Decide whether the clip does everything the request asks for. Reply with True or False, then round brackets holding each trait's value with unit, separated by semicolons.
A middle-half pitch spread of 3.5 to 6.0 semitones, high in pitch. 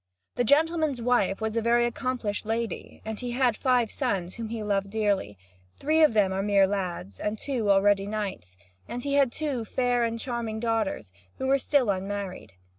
True (3.8 semitones; 220 Hz)